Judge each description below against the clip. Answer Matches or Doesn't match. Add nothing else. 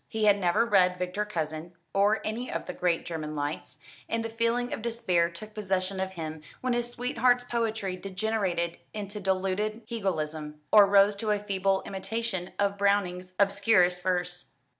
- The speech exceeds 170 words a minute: Doesn't match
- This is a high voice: Matches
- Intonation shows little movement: Doesn't match